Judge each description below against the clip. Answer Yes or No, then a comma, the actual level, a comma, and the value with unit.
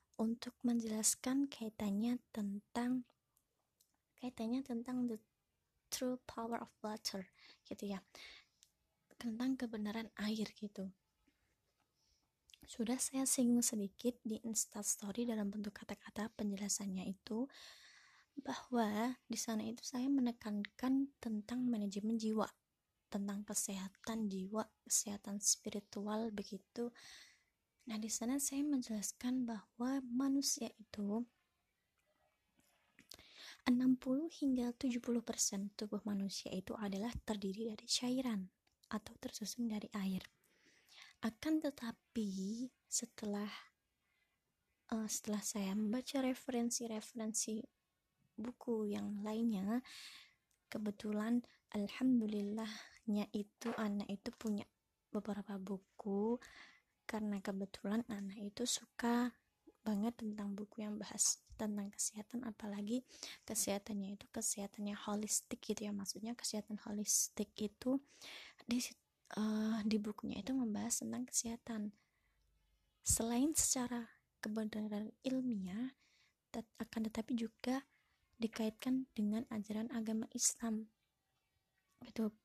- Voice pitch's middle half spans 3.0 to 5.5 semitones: No, narrow, 2.6 semitones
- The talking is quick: No, average, 95 wpm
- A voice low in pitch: No, high, 225 Hz